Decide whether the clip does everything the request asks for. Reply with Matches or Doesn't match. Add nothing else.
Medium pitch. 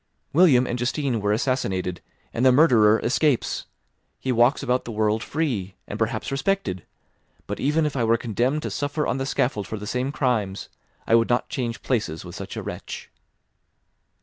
Doesn't match